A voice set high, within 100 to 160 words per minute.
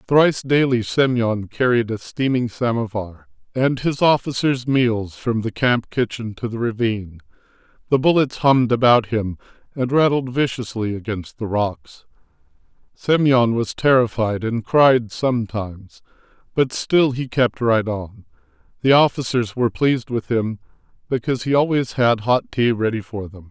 No: low, 120 Hz; average, 145 wpm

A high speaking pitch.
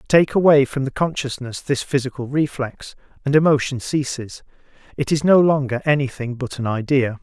No: low, 135 Hz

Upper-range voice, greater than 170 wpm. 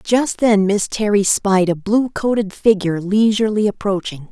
No: high, 205 Hz; average, 155 wpm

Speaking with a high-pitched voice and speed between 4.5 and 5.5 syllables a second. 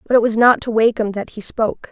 No: high, 225 Hz; 6.5 syllables/s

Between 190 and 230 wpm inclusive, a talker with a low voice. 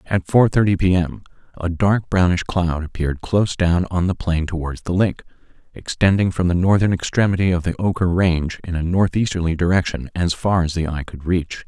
Yes: average, 195 wpm; very low, 90 Hz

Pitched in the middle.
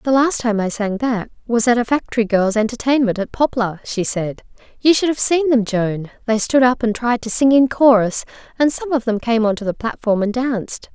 No: high, 235 Hz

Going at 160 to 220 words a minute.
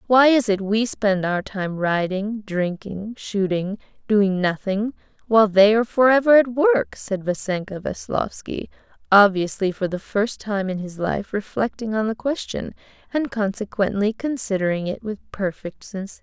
No: average, 150 wpm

